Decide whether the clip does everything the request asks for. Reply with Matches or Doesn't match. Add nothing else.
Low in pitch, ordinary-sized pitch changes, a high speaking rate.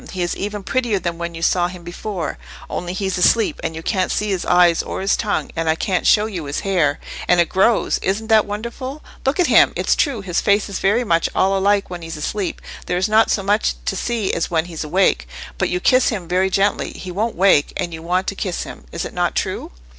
Doesn't match